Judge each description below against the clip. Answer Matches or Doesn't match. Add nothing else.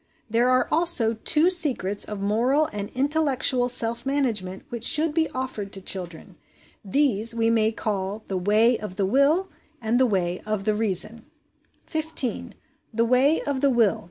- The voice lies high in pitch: Matches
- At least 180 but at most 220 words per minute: Doesn't match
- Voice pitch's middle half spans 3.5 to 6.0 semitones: Matches